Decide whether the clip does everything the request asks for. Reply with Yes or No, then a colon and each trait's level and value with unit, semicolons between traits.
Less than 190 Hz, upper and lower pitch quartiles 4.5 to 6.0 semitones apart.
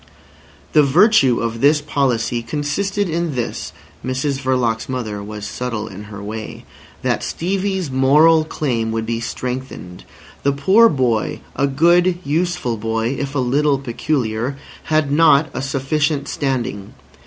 Yes: low, 135 Hz; average, 4.8 semitones